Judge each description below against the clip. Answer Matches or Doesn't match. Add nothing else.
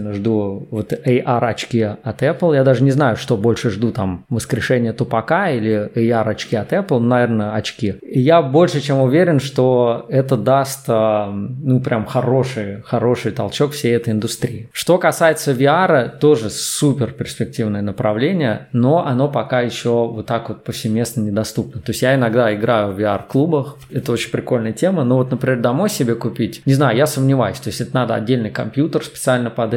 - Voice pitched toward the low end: Matches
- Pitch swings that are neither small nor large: Matches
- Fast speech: Matches